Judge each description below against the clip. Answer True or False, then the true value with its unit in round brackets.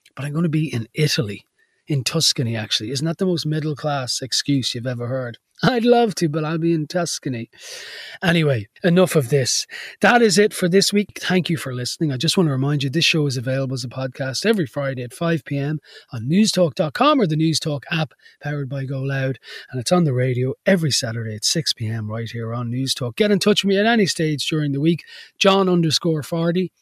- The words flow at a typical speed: False (215 wpm)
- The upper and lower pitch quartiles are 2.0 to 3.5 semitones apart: False (4.8 semitones)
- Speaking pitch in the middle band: True (150 Hz)